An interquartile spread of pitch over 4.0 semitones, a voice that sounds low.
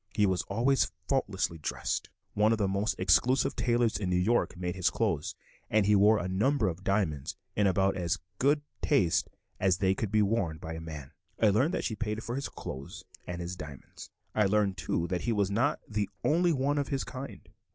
Yes: average, 4.4 semitones; low, 100 Hz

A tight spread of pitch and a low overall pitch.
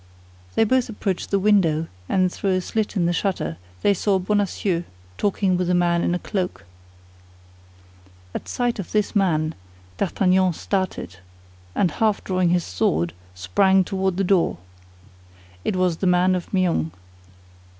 No: narrow, 2.3 semitones; medium, 185 Hz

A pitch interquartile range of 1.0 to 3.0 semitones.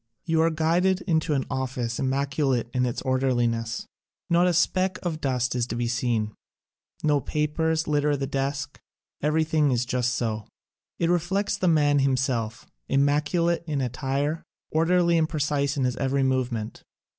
No: average, 4.1 semitones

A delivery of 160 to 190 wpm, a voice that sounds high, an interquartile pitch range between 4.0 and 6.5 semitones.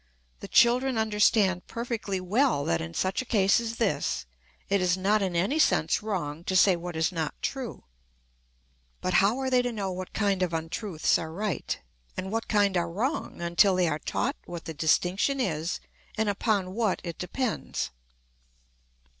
Yes: average, 170 wpm; high, 195 Hz; average, 4.3 semitones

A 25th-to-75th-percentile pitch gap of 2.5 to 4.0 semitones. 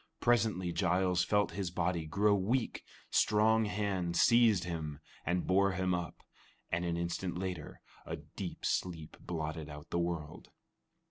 Yes: average, 2.8 semitones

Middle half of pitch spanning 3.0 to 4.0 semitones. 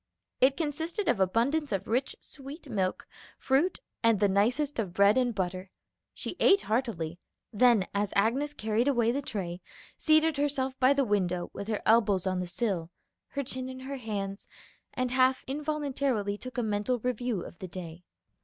No: average, 5.3 semitones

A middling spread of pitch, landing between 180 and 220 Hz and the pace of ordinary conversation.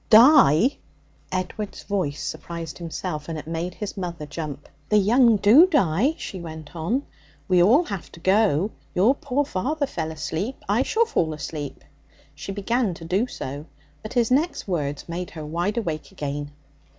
No: wide, 6.5 semitones; medium, 185 Hz; average, 160 wpm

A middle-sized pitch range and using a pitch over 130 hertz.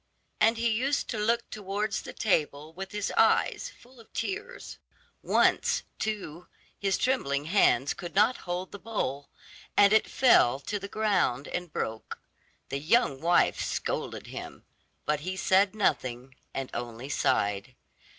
No: wide, 7.4 semitones; high, 190 Hz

